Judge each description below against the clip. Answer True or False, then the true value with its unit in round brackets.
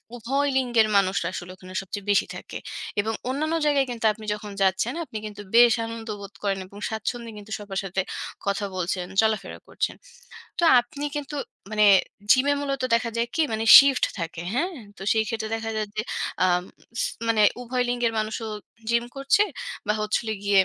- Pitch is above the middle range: True (220 Hz)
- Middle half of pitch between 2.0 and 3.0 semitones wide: False (3.4 semitones)